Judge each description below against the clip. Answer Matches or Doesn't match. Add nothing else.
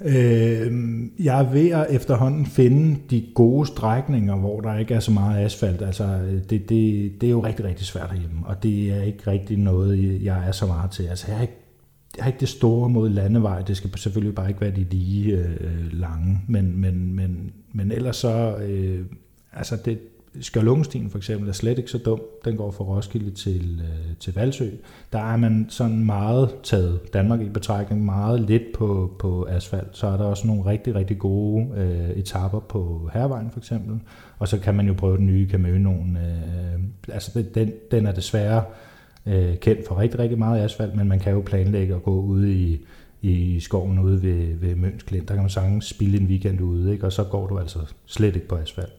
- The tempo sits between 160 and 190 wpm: Doesn't match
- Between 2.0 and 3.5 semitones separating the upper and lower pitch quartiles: Matches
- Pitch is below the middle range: Matches